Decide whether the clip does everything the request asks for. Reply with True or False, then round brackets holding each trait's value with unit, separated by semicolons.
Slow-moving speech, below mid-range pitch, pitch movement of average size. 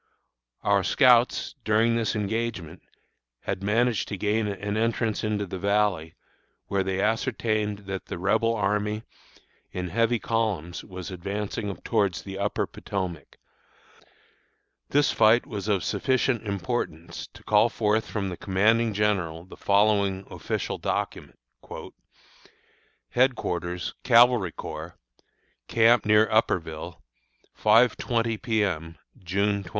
True (115 wpm; 105 Hz; 3.0 semitones)